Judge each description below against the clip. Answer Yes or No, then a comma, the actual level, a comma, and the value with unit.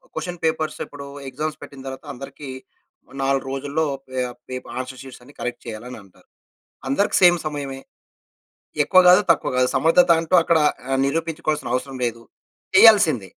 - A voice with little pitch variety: No, average, 3.8 semitones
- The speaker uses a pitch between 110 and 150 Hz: Yes, medium, 140 Hz